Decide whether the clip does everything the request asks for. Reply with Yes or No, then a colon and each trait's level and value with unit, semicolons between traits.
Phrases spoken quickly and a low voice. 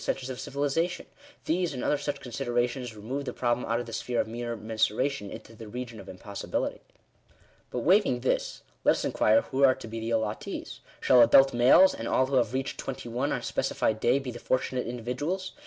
Yes: fast, 220 wpm; low, 125 Hz